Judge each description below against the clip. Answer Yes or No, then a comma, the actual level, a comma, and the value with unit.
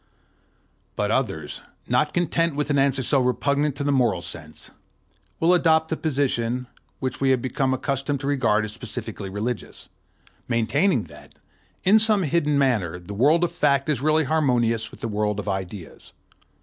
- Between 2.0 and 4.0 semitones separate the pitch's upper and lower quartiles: No, average, 5.2 semitones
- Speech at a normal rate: Yes, average, 160 wpm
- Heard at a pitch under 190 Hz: Yes, low, 135 Hz